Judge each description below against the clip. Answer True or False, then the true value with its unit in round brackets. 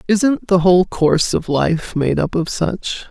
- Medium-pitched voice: True (180 Hz)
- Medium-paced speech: True (195 wpm)